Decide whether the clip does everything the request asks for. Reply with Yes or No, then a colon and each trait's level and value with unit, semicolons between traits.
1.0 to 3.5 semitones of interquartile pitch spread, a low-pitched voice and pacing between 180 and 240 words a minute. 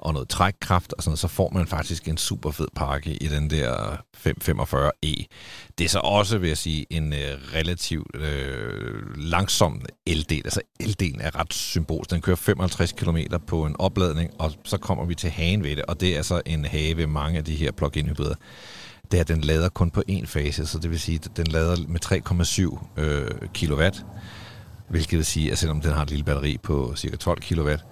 Yes: average, 3.1 semitones; very low, 80 Hz; average, 210 wpm